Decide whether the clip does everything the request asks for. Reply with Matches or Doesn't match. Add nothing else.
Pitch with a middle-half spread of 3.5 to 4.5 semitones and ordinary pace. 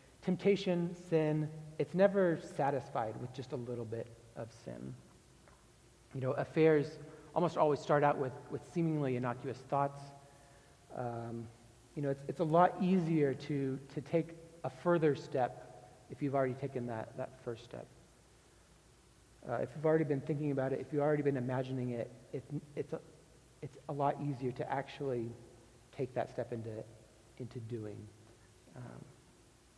Matches